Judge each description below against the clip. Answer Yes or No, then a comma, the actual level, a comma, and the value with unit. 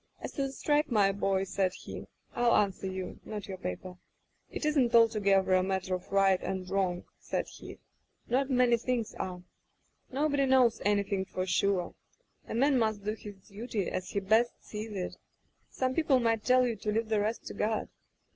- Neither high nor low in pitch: No, high, 210 Hz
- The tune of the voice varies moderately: Yes, average, 4.0 semitones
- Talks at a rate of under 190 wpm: No, average, 195 wpm